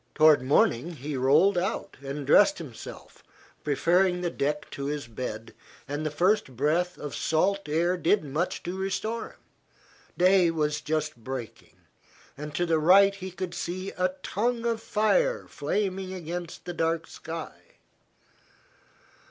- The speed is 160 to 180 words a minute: No, average, 145 wpm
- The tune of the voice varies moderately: Yes, average, 4.1 semitones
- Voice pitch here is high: No, medium, 170 Hz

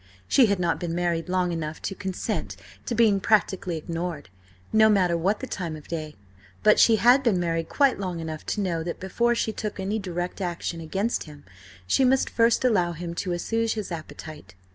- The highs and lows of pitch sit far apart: No, average, 4.5 semitones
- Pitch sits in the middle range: Yes, medium, 180 Hz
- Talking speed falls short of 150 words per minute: No, average, 195 wpm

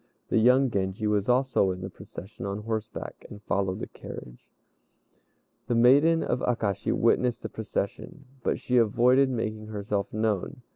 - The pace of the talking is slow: No, average, 150 wpm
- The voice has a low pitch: Yes, low, 110 Hz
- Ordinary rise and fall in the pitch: Yes, average, 3.7 semitones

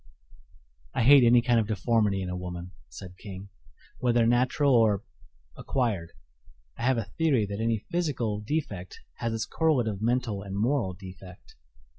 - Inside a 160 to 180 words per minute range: No, average, 150 wpm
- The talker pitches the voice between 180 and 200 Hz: No, low, 110 Hz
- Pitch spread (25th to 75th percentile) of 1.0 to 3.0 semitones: No, average, 3.9 semitones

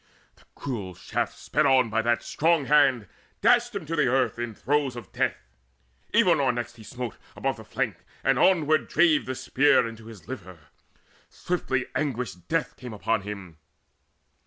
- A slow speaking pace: No, average, 160 wpm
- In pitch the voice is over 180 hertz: No, low, 130 Hz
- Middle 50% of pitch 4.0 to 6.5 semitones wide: Yes, average, 5.0 semitones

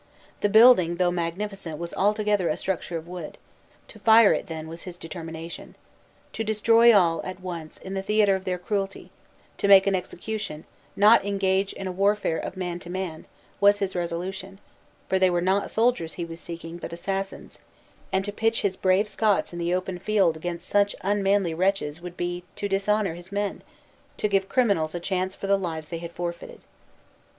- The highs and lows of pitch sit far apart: No, average, 2.8 semitones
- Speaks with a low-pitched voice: No, high, 190 Hz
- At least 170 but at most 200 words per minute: Yes, average, 185 wpm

